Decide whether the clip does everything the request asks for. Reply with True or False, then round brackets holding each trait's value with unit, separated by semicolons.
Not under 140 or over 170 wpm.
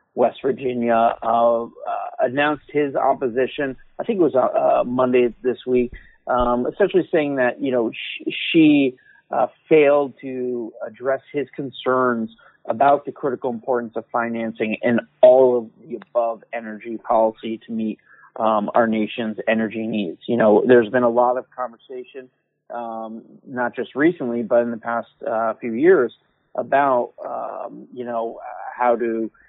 True (155 wpm)